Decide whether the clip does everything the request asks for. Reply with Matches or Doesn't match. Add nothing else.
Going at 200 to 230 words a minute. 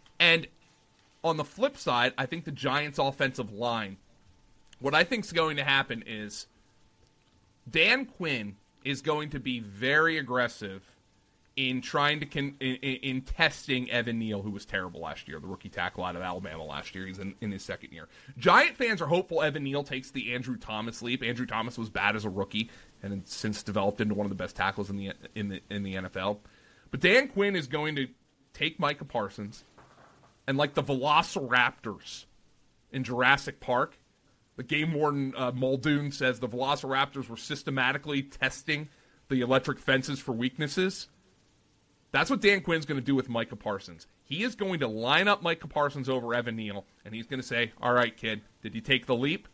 Doesn't match